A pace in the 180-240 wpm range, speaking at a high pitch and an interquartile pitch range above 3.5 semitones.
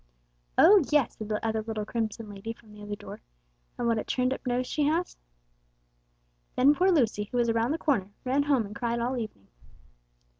Yes: average, 195 wpm; high, 235 Hz; average, 3.9 semitones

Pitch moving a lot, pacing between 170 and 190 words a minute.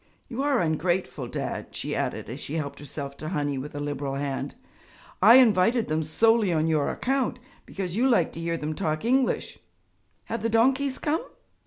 Yes: wide, 7.6 semitones; average, 180 wpm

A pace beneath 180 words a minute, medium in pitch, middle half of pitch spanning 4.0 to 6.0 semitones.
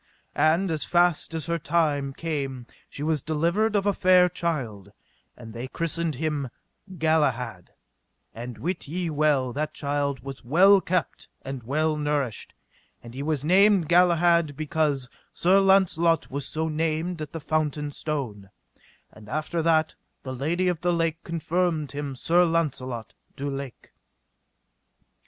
No: average, 140 wpm; medium, 155 Hz; average, 3.5 semitones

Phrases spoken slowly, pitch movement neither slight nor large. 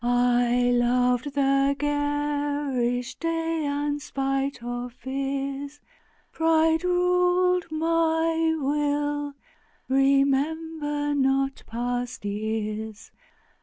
Yes: slow, 75 wpm; average, 4.0 semitones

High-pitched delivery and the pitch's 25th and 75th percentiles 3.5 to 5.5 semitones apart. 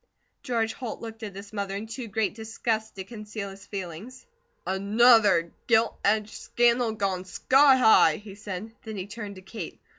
No: high, 215 Hz; narrow, 2.4 semitones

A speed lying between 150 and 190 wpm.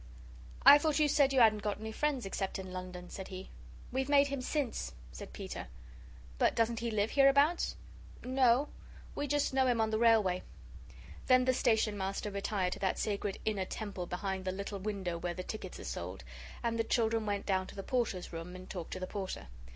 No: average, 200 wpm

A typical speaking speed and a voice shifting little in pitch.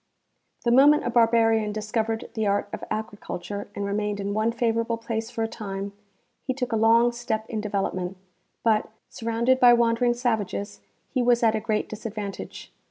Yes: average, 170 wpm; narrow, 2.1 semitones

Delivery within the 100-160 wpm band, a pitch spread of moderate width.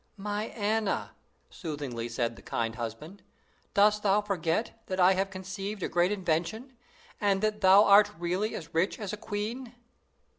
Yes: average, 155 wpm; average, 3.9 semitones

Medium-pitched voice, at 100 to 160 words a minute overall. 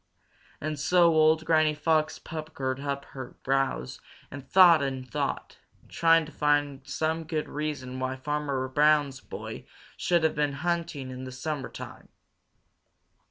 Yes: medium, 150 Hz; slow, 135 wpm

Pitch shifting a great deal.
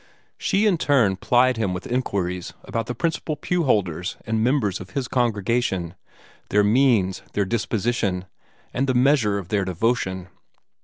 No: average, 5.0 semitones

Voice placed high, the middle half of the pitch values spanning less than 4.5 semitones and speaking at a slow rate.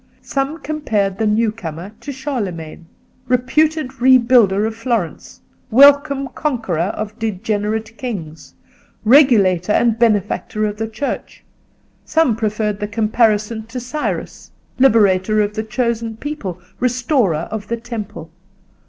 Yes: high, 225 Hz; average, 3.5 semitones; slow, 120 wpm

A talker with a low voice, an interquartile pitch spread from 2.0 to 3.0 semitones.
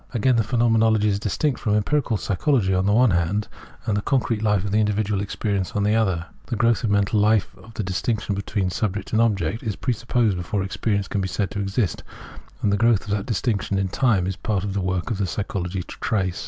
Yes: low, 105 Hz; narrow, 2.6 semitones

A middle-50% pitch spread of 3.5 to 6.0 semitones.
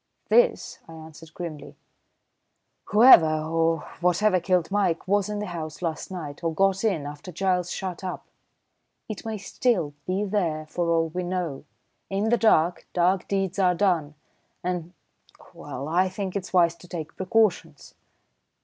No: average, 3.0 semitones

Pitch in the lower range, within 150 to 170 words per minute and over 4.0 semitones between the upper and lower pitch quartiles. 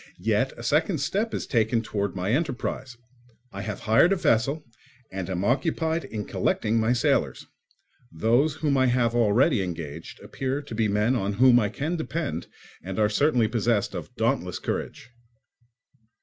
Yes: low, 115 Hz; average, 160 wpm; average, 4.9 semitones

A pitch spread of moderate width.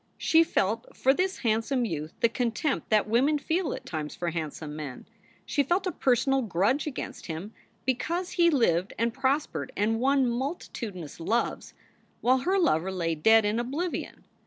No: wide, 6.9 semitones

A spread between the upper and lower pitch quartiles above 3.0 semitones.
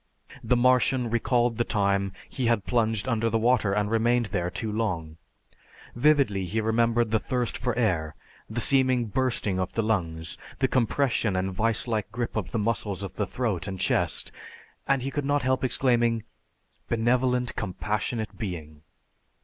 Yes: average, 3.5 semitones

